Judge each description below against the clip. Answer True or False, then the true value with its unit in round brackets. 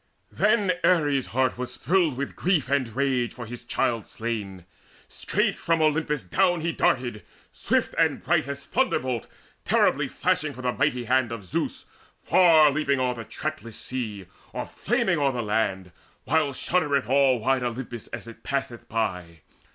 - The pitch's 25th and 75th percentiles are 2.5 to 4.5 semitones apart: True (4.1 semitones)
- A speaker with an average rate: True (160 wpm)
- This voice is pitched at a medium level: False (130 Hz)